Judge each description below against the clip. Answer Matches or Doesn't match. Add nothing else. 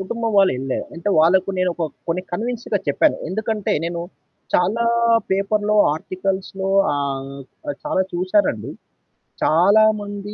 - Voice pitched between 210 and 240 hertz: Doesn't match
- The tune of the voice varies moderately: Matches